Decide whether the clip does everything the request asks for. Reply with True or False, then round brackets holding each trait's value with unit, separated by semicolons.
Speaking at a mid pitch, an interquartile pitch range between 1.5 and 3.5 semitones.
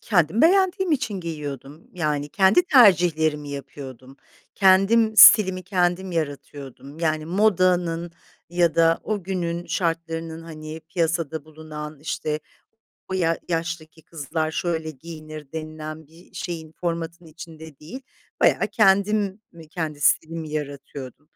True (165 Hz; 2.9 semitones)